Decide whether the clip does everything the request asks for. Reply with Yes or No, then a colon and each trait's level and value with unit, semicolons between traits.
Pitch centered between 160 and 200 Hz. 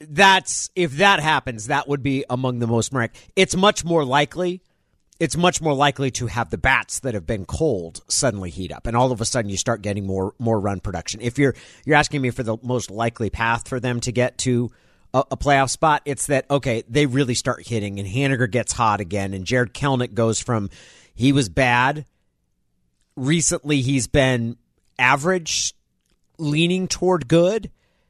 No: low, 125 Hz